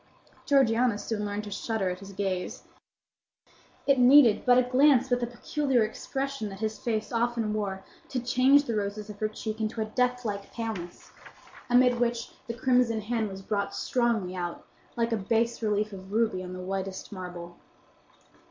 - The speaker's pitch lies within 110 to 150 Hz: No, high, 220 Hz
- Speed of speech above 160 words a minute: Yes, average, 170 wpm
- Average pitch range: Yes, average, 3.4 semitones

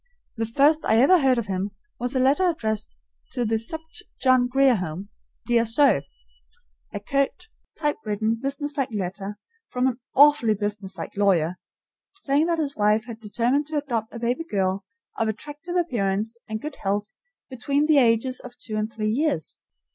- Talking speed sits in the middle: Yes, average, 160 wpm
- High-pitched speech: Yes, high, 235 Hz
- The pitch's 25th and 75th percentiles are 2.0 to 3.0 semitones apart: No, average, 5.0 semitones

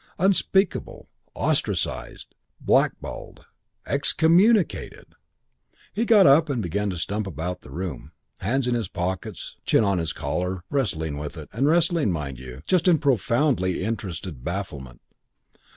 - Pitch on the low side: Yes, low, 100 Hz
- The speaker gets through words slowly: Yes, slow, 130 wpm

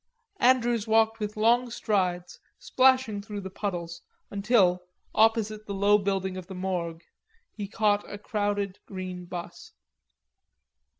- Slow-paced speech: Yes, slow, 125 wpm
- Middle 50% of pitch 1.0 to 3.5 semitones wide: Yes, average, 2.9 semitones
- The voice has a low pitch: No, high, 205 Hz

